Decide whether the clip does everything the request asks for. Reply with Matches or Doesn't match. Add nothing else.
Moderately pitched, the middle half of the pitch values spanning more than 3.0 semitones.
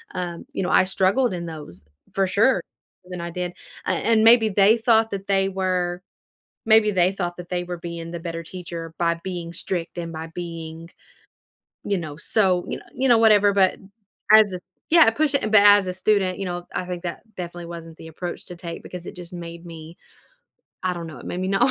Doesn't match